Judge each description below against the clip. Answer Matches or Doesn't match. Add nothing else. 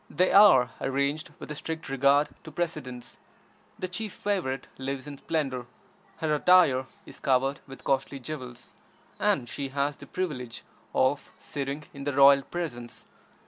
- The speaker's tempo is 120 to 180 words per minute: Matches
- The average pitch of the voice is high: Doesn't match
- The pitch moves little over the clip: Doesn't match